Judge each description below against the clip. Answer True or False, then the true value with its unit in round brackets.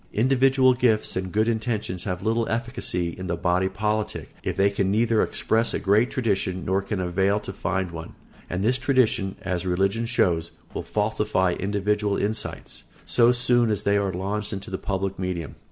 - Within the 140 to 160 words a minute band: False (170 wpm)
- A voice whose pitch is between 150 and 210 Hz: False (100 Hz)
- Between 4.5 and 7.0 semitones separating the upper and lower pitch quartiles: False (3.4 semitones)